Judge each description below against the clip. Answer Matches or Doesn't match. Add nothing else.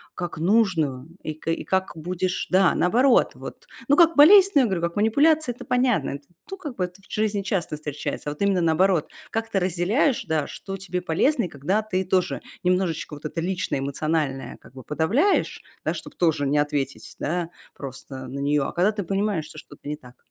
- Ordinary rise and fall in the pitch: Doesn't match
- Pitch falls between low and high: Matches